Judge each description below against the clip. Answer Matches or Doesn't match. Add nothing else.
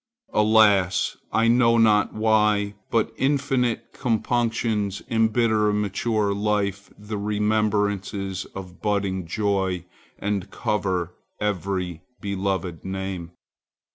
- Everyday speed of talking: Doesn't match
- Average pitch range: Doesn't match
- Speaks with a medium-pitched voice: Doesn't match